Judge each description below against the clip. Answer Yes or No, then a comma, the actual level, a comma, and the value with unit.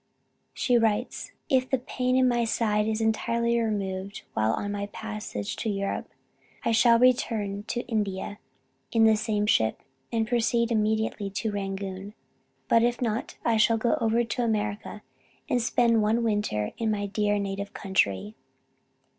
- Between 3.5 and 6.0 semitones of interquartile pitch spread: No, narrow, 2.4 semitones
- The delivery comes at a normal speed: Yes, average, 155 wpm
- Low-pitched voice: No, high, 220 Hz